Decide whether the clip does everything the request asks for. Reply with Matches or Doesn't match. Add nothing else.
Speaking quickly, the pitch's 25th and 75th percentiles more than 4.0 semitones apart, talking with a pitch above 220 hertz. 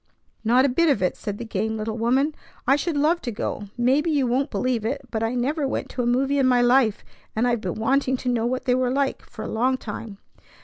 Doesn't match